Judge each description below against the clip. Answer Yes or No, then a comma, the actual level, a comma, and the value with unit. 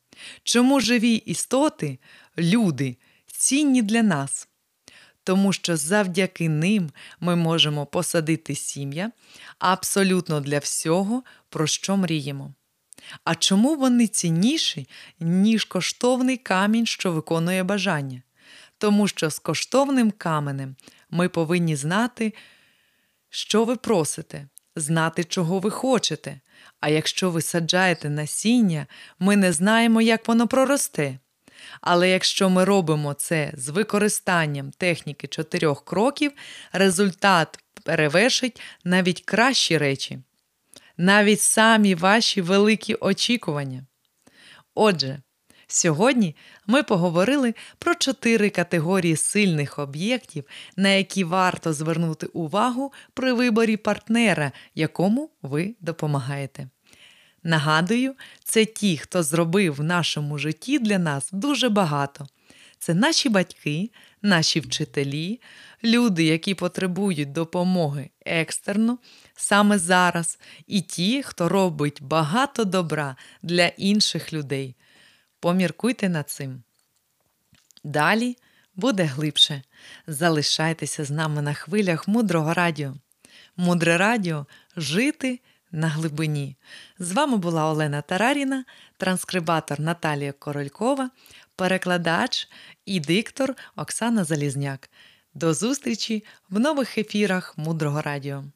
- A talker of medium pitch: Yes, medium, 180 Hz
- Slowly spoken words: Yes, slow, 100 wpm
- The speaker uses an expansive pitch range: Yes, wide, 5.7 semitones